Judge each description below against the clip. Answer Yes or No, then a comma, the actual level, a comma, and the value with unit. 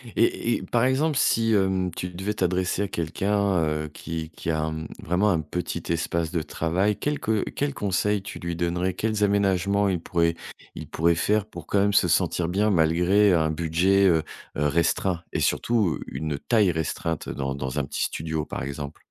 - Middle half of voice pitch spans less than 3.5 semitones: No, average, 3.9 semitones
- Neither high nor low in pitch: No, very low, 90 Hz